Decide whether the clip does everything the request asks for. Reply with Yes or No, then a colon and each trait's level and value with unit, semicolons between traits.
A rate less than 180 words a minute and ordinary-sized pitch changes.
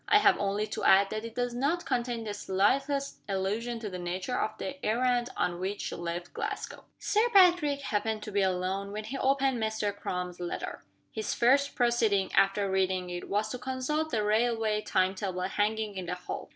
No: average, 190 wpm; average, 4.5 semitones